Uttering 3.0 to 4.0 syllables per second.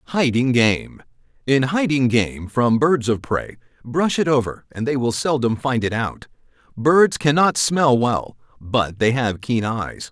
Yes: 3.9 syllables/s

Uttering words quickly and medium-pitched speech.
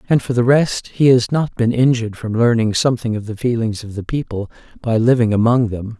No: fast, 220 wpm; low, 115 Hz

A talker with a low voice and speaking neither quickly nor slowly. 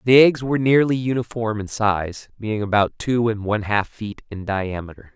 Yes: low, 110 Hz; average, 185 wpm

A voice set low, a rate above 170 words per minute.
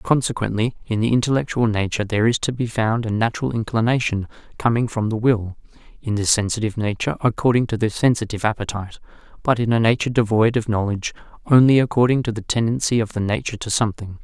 Yes: low, 115 Hz; average, 180 wpm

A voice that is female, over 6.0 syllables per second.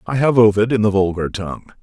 No: male; 6.6 syllables/s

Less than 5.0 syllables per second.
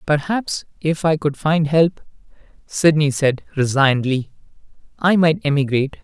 Yes: 4.6 syllables/s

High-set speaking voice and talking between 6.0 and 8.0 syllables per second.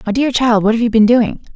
Yes: high, 230 Hz; 6.2 syllables/s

